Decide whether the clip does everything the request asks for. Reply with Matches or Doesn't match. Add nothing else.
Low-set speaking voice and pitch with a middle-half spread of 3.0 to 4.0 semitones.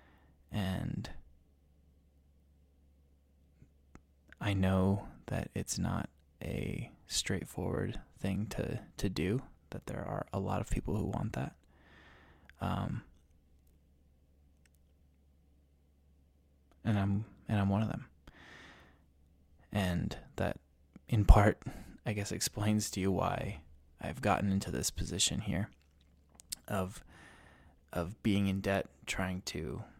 Doesn't match